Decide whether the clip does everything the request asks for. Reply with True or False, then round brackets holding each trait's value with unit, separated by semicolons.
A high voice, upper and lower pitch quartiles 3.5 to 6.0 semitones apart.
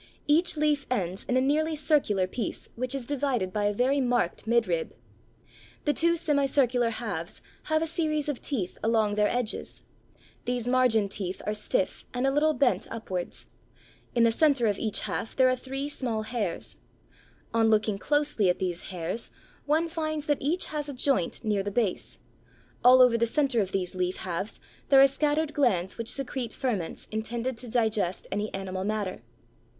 True (240 Hz; 5.4 semitones)